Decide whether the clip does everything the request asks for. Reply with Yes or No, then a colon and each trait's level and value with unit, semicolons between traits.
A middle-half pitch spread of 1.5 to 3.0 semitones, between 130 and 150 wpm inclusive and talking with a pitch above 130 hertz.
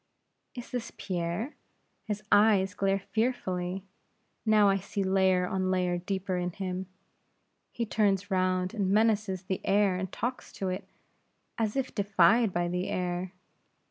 Yes: narrow, 2.4 semitones; average, 140 wpm; high, 190 Hz